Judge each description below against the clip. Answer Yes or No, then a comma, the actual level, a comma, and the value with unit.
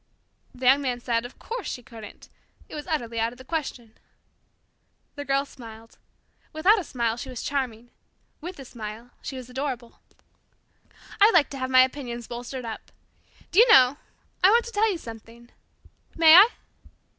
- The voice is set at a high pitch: Yes, very high, 255 Hz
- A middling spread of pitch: Yes, average, 4.6 semitones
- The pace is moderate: Yes, average, 170 wpm